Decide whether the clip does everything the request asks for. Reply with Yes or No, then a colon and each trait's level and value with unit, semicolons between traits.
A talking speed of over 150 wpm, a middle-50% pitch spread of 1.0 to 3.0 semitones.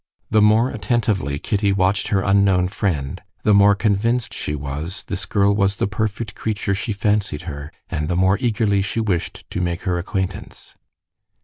Yes: average, 170 wpm; average, 2.7 semitones